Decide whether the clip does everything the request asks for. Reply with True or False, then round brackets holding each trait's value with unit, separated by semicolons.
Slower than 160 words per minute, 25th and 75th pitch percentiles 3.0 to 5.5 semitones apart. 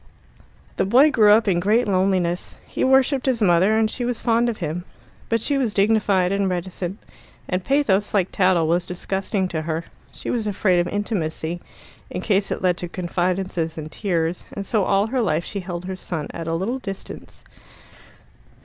False (185 wpm; 3.8 semitones)